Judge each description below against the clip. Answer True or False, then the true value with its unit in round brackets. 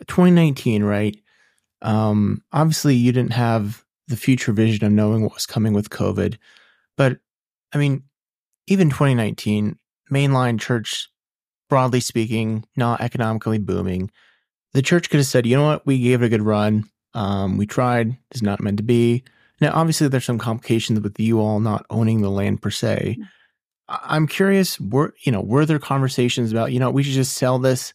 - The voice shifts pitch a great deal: False (3.9 semitones)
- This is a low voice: True (120 Hz)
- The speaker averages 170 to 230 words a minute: True (175 wpm)